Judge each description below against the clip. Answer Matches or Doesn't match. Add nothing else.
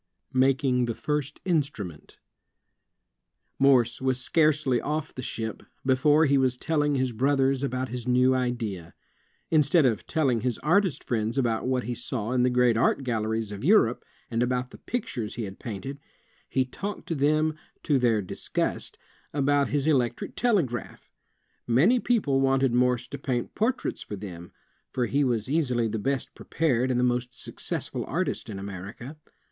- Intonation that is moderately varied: Matches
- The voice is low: Matches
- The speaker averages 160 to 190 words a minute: Matches